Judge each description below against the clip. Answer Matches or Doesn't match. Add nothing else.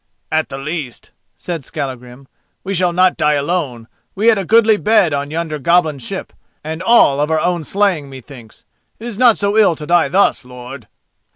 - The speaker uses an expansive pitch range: Matches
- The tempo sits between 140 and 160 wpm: Doesn't match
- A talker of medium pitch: Matches